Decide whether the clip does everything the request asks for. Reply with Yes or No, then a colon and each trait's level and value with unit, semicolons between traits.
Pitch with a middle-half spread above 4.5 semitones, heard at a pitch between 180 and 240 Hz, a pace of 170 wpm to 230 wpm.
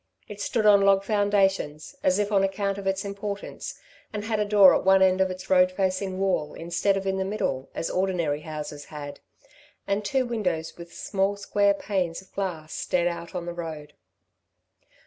No: average, 2.7 semitones; high, 190 Hz; average, 185 wpm